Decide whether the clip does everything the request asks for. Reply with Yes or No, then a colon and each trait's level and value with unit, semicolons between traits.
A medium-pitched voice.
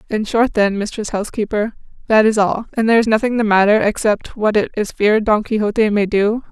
No: high, 215 Hz